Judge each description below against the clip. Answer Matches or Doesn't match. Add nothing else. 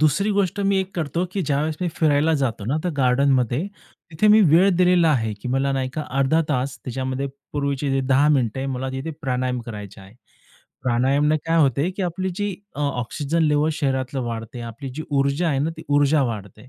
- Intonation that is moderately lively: Matches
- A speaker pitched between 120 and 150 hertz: Matches